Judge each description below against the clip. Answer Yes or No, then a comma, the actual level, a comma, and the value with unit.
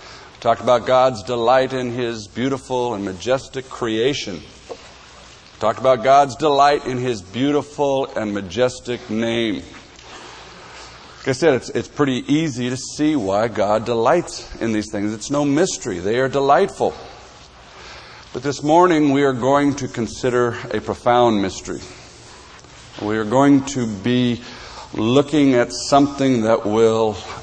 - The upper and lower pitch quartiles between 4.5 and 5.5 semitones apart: No, average, 3.4 semitones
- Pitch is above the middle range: No, low, 125 Hz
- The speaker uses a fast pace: No, slow, 135 wpm